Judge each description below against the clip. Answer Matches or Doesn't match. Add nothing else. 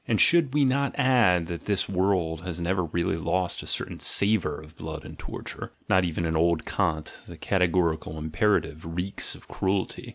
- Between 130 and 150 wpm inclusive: Doesn't match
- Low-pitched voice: Matches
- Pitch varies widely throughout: Doesn't match